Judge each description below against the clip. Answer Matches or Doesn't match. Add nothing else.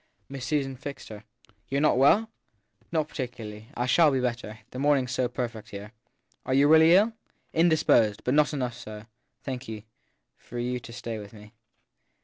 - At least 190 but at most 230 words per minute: Matches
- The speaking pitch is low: Matches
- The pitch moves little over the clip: Doesn't match